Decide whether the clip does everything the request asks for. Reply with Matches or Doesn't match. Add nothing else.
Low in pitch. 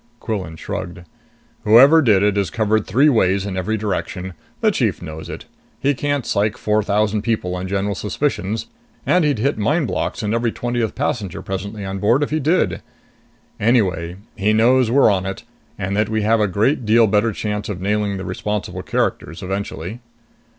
Matches